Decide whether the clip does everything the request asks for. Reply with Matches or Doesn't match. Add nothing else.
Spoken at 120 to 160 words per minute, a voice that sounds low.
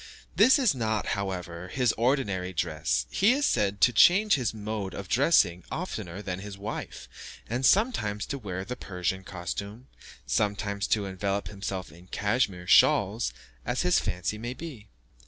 Matches